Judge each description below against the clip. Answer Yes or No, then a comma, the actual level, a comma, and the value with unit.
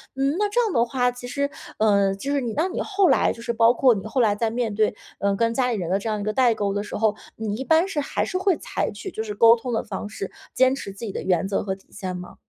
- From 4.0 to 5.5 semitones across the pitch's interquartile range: Yes, average, 4.7 semitones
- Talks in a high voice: Yes, high, 230 Hz